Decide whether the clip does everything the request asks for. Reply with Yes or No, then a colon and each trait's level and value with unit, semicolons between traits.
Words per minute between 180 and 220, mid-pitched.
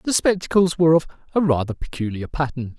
No: average, 170 wpm; medium, 155 Hz